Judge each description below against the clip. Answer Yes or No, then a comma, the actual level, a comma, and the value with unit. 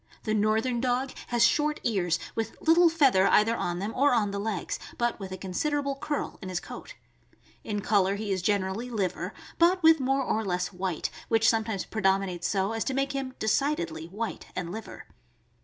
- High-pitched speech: Yes, high, 220 Hz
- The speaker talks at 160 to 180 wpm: No, average, 190 wpm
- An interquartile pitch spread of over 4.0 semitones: Yes, average, 5.3 semitones